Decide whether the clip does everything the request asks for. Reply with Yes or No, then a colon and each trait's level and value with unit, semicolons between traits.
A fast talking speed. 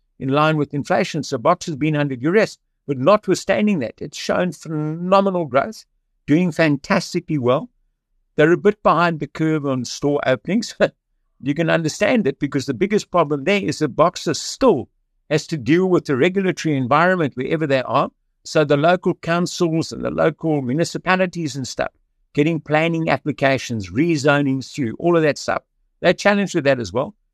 No: average, 170 wpm